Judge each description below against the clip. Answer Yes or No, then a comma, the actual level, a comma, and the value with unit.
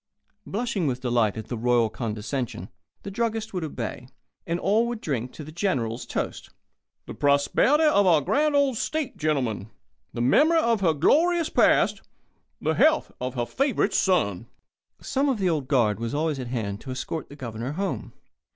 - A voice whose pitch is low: No, medium, 150 Hz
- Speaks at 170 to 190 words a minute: Yes, average, 175 wpm